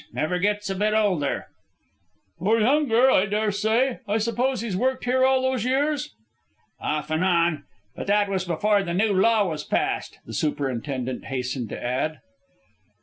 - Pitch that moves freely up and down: Yes, wide, 6.7 semitones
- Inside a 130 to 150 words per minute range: No, average, 160 wpm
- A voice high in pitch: Yes, high, 205 Hz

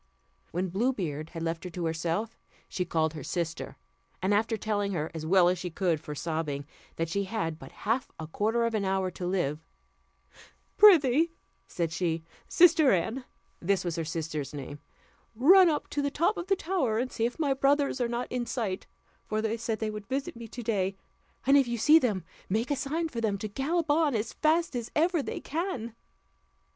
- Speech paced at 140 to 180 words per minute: No, average, 200 wpm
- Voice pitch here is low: No, high, 215 Hz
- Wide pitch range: Yes, wide, 7.8 semitones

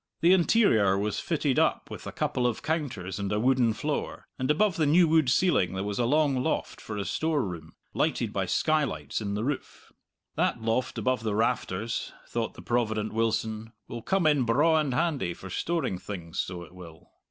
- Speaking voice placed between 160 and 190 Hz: No, low, 120 Hz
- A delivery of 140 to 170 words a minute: No, average, 190 wpm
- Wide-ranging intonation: Yes, wide, 6.7 semitones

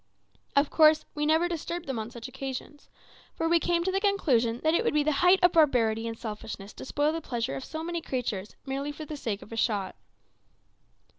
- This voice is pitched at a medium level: No, very high, 285 Hz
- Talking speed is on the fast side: Yes, fast, 215 wpm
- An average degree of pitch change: No, wide, 5.8 semitones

